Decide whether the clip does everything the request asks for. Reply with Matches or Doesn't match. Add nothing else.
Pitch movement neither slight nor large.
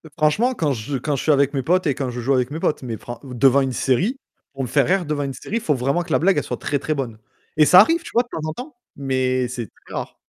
Matches